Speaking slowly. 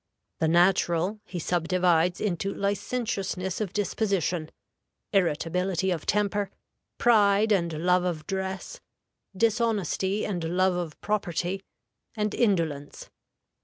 Yes: slow, 100 wpm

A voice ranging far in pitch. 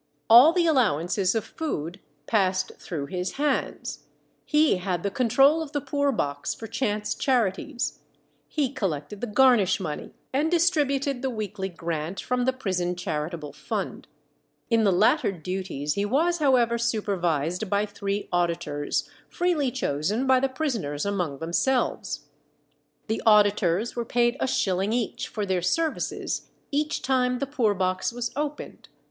Yes: wide, 6.4 semitones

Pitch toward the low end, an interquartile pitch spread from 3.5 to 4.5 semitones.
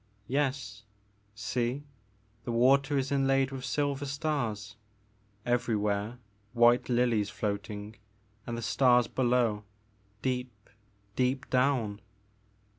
Yes: low, 120 Hz; average, 4.0 semitones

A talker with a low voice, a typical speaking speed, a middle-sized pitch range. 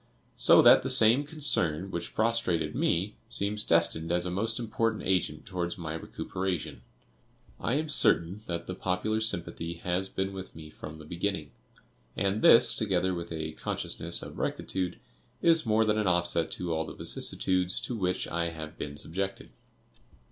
Yes: very low, 90 Hz; average, 160 wpm; average, 4.1 semitones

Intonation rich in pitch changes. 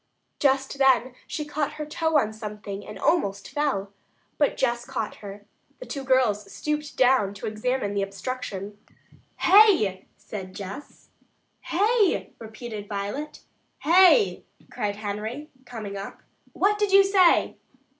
Yes: wide, 6.7 semitones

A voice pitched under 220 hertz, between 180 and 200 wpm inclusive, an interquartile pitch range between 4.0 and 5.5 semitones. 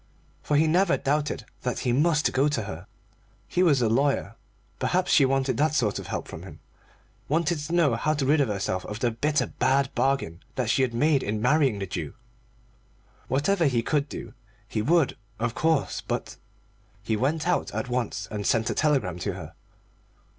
Yes: low, 135 Hz; average, 185 wpm; average, 5.0 semitones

